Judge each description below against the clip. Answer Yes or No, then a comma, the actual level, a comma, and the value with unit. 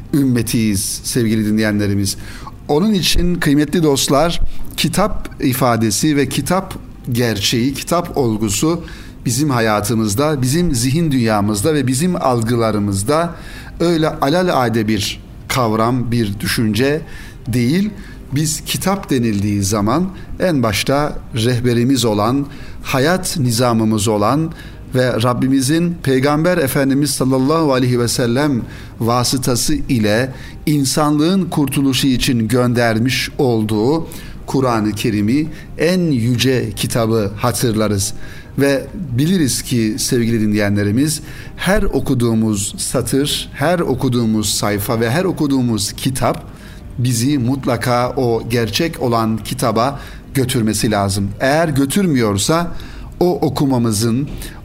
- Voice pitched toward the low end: Yes, low, 125 Hz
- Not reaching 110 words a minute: Yes, average, 100 wpm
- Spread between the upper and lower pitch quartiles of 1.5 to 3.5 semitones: No, average, 4.6 semitones